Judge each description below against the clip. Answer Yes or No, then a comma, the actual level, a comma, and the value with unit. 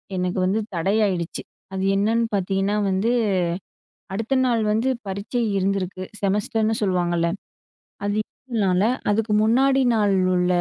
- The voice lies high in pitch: Yes, high, 200 Hz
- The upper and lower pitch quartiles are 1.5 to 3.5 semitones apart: Yes, average, 2.9 semitones